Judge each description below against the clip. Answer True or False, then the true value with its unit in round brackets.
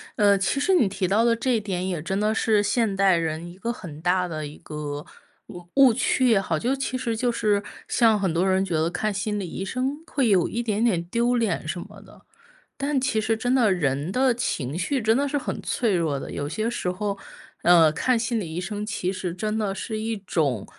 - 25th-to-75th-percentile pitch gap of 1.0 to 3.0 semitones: False (4.7 semitones)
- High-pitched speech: True (205 Hz)